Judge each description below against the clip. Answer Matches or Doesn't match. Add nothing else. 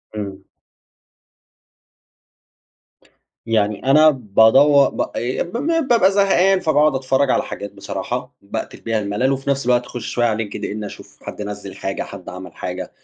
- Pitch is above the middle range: Doesn't match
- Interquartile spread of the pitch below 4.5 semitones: Doesn't match